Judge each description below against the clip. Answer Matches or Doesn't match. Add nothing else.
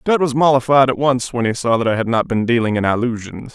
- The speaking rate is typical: Doesn't match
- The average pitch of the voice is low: Matches